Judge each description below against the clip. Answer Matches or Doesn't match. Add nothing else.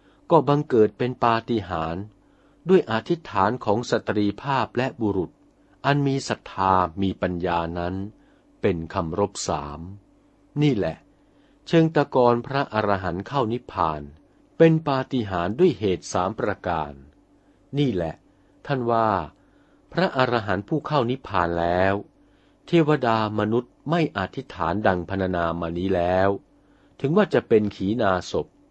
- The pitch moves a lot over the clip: Matches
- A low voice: Matches